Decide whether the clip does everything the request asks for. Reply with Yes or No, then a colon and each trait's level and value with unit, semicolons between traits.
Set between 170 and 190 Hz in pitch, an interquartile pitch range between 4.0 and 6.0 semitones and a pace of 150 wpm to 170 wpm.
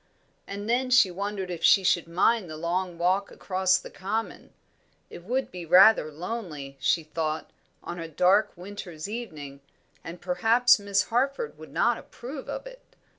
Yes: medium, 185 Hz; average, 4.7 semitones; average, 160 wpm